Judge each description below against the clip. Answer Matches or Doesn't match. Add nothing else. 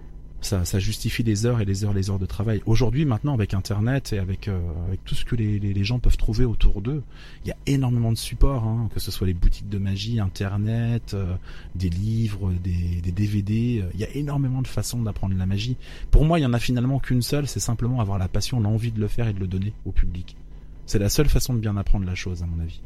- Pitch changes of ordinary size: Matches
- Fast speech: Matches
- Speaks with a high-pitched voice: Doesn't match